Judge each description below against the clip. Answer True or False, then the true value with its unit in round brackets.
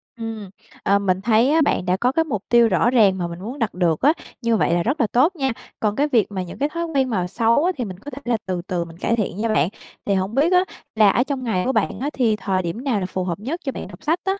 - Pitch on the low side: False (225 Hz)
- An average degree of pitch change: False (6.1 semitones)